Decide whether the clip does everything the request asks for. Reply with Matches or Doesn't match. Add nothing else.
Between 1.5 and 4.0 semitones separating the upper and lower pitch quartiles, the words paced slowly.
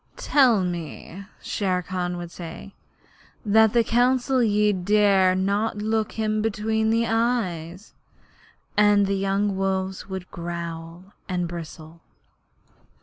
Matches